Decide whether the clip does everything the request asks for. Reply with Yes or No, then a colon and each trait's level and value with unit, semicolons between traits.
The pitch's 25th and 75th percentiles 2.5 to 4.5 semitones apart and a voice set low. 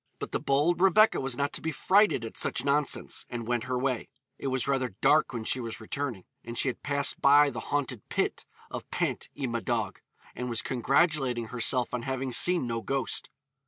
Yes: average, 3.1 semitones; low, 130 Hz